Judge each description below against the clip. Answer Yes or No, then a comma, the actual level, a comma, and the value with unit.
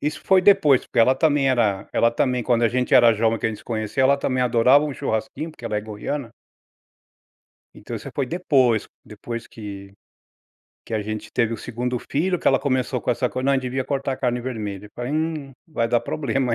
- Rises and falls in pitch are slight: No, average, 3.2 semitones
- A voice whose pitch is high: No, low, 125 Hz